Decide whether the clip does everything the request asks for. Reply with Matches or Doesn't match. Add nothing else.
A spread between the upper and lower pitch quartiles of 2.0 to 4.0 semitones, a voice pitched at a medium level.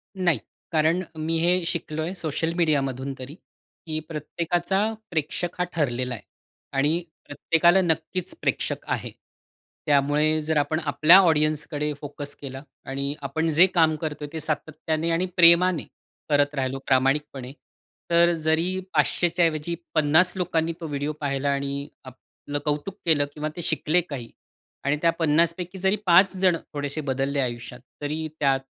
Matches